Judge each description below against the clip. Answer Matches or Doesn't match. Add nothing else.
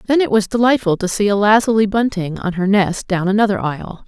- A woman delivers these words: Matches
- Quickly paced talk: Matches